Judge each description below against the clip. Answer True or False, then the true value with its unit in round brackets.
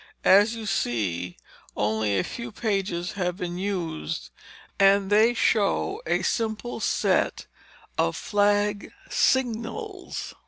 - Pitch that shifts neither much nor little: True (4.5 semitones)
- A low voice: False (205 Hz)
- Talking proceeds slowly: True (110 wpm)